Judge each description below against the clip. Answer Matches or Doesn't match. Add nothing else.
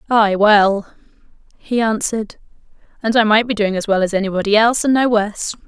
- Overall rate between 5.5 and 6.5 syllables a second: Matches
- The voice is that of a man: Doesn't match